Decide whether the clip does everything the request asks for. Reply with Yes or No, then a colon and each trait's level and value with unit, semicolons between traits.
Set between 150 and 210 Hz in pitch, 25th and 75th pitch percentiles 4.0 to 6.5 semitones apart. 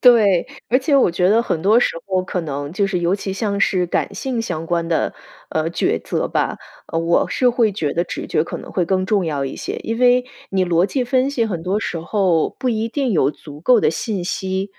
Yes: high, 190 Hz; average, 5.1 semitones